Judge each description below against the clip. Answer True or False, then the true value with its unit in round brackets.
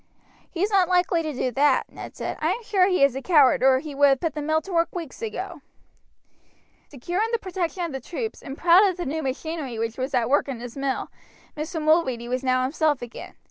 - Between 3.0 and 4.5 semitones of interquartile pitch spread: False (5.1 semitones)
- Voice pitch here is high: True (305 Hz)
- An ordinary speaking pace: False (230 wpm)